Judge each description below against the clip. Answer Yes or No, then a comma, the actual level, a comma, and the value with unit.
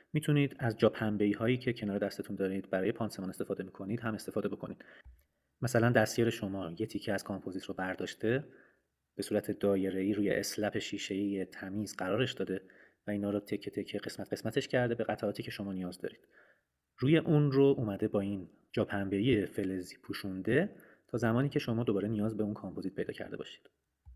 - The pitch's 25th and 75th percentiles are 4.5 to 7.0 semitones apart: No, average, 3.0 semitones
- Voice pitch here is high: No, low, 105 Hz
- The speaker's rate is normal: No, fast, 170 wpm